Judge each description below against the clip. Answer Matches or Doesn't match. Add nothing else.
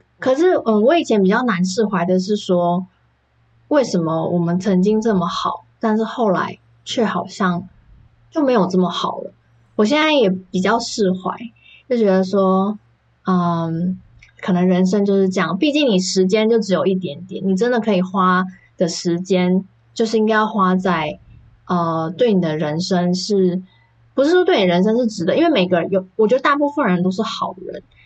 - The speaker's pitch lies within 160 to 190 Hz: Matches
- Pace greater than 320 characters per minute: Doesn't match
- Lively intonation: Doesn't match